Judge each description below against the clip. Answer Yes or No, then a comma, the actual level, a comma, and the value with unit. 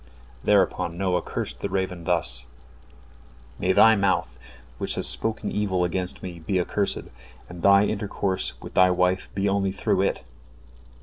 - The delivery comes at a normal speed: Yes, average, 150 wpm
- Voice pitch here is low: Yes, very low, 95 Hz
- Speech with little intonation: Yes, narrow, 1.9 semitones